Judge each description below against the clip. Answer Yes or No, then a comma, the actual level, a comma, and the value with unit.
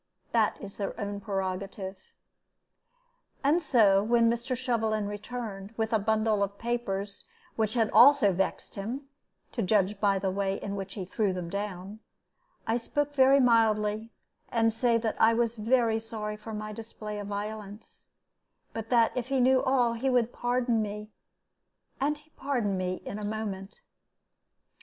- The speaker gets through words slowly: No, average, 155 wpm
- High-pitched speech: Yes, high, 220 Hz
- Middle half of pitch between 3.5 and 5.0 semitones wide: No, average, 2.8 semitones